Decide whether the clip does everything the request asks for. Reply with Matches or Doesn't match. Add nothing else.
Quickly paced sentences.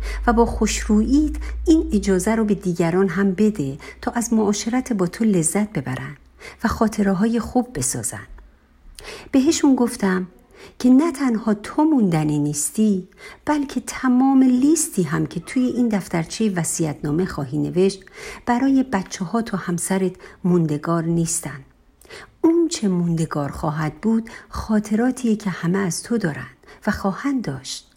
Doesn't match